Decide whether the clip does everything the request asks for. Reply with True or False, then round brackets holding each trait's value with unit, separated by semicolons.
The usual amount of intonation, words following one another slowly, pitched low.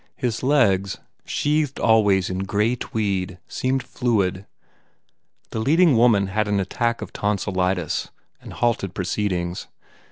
True (4.1 semitones; 125 wpm; 105 Hz)